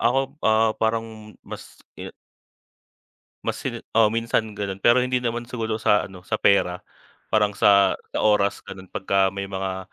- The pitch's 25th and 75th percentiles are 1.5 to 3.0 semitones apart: Yes, average, 2.7 semitones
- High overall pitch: No, low, 105 Hz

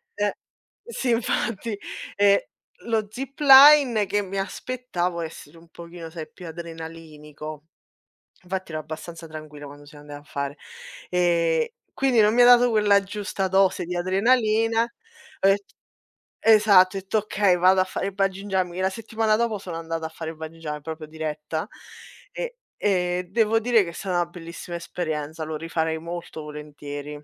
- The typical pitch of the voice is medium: Yes, medium, 180 Hz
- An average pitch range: Yes, average, 4.7 semitones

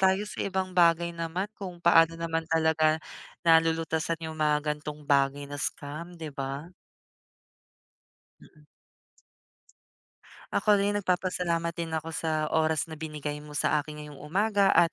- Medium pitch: Yes, medium, 160 Hz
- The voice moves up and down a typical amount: No, narrow, 2.2 semitones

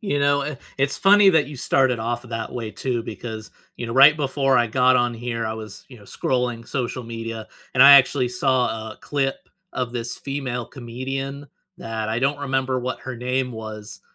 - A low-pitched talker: Yes, low, 125 Hz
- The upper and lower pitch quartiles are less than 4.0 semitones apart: Yes, average, 2.8 semitones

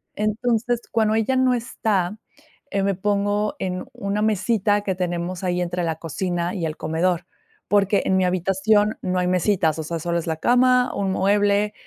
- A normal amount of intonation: Yes, average, 3.0 semitones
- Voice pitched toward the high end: Yes, high, 195 Hz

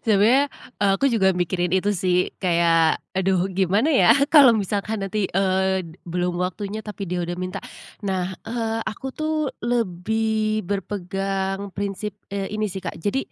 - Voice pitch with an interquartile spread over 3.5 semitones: No, average, 2.9 semitones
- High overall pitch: Yes, high, 195 Hz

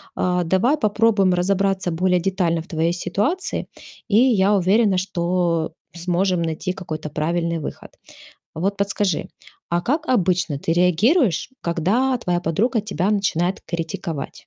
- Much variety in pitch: No, average, 3.2 semitones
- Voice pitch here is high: No, medium, 180 Hz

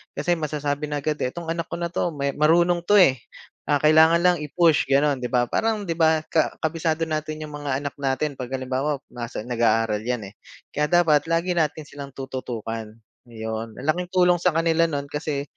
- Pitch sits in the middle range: Yes, medium, 150 Hz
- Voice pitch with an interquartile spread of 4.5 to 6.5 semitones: No, average, 3.7 semitones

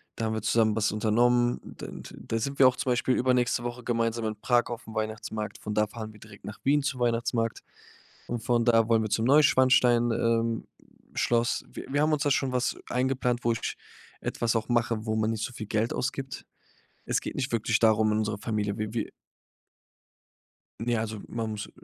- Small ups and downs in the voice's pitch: Yes, narrow, 2.0 semitones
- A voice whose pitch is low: Yes, low, 115 Hz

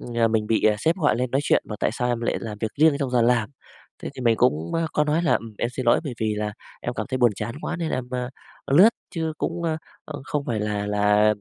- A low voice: Yes, low, 120 Hz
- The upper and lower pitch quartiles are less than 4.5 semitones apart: No, average, 5.2 semitones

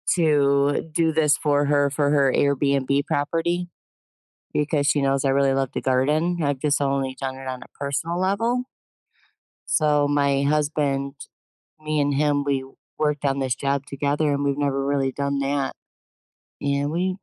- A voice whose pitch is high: No, medium, 145 Hz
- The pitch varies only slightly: Yes, narrow, 1.5 semitones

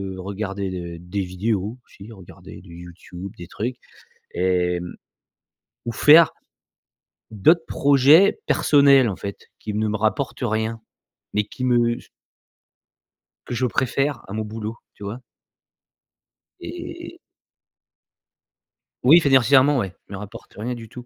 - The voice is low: Yes, low, 110 Hz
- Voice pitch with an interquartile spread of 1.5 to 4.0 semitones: No, average, 4.8 semitones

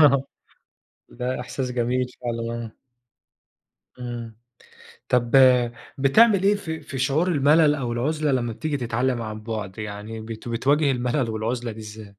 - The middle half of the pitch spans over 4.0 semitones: No, average, 3.6 semitones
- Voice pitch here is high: No, low, 125 Hz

